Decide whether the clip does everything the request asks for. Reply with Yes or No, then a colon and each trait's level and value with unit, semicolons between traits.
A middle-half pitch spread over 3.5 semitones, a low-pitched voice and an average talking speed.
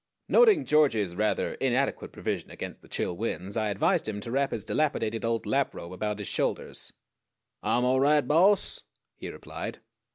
Yes: wide, 5.6 semitones; low, 115 Hz; average, 165 wpm